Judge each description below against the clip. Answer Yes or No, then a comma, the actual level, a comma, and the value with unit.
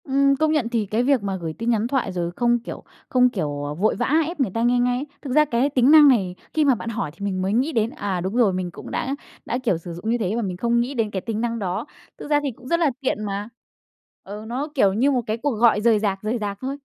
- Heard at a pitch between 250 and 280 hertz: No, high, 230 Hz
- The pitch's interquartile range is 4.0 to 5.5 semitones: Yes, average, 4.5 semitones